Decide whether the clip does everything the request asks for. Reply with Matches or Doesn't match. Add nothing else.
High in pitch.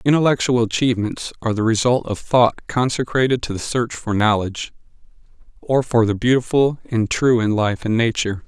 Doesn't match